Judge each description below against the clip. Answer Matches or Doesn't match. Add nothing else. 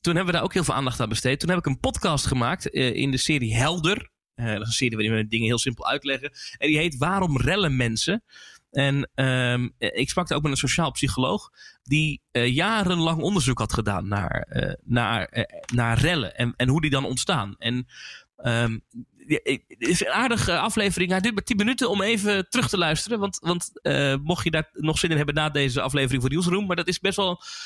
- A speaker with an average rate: Doesn't match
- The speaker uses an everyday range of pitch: Doesn't match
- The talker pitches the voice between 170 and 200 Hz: Doesn't match